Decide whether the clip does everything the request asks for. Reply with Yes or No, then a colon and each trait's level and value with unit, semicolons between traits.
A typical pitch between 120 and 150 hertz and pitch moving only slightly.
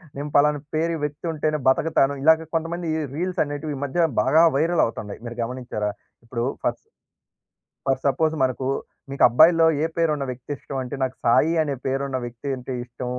No: medium, 140 Hz; average, 3.8 semitones